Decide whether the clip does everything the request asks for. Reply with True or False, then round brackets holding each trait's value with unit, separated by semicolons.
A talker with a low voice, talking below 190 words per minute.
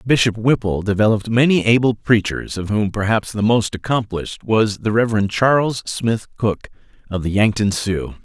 True (110 Hz; 160 wpm)